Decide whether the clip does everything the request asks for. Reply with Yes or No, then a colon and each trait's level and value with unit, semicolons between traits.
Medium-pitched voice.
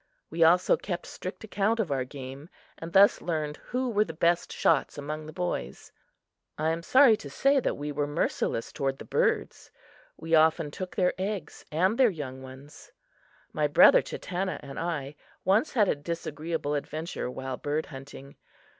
Yes: medium, 160 Hz